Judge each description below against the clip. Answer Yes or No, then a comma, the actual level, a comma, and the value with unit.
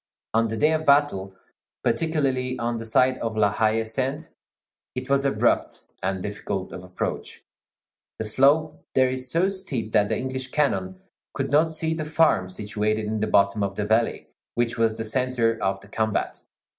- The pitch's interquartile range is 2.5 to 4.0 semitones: No, average, 4.6 semitones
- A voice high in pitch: No, low, 115 Hz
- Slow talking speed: No, average, 175 wpm